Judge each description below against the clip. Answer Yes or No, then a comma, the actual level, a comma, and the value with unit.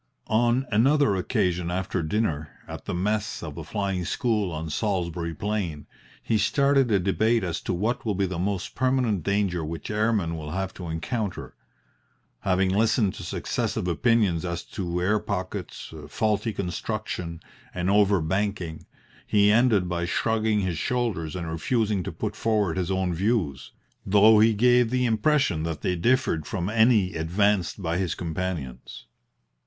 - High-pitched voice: No, very low, 95 Hz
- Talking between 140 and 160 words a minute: Yes, average, 155 wpm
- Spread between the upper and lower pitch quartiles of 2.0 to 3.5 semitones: No, average, 4.0 semitones